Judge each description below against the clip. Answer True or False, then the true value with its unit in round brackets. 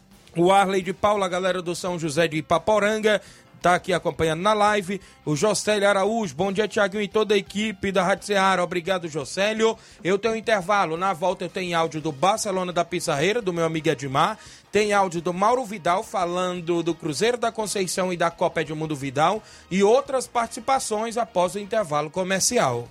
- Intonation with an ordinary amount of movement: True (3.8 semitones)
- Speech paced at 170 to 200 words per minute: True (185 wpm)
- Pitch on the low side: False (190 Hz)